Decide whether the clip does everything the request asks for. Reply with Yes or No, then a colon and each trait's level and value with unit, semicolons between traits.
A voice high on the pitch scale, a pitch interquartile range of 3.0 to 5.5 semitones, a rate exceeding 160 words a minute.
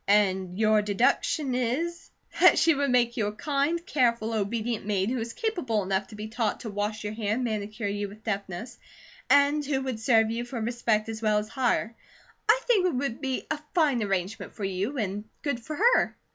Yes: high, 225 Hz; average, 4.3 semitones; fast, 205 wpm